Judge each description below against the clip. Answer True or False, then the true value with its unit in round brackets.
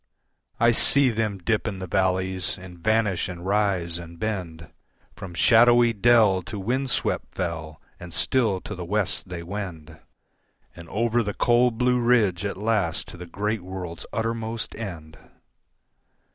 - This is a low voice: True (100 Hz)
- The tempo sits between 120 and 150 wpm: True (145 wpm)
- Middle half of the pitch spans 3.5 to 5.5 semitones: True (4.3 semitones)